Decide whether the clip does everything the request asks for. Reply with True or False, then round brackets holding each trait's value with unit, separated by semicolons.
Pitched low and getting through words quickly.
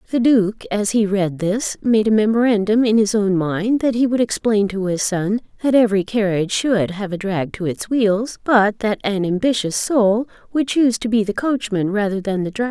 False (210 Hz; 210 wpm)